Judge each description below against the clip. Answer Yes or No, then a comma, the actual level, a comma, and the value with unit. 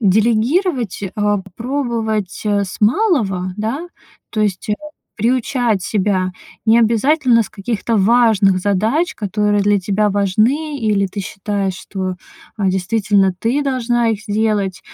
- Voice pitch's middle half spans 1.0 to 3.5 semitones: Yes, average, 3.1 semitones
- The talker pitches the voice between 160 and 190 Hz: No, high, 215 Hz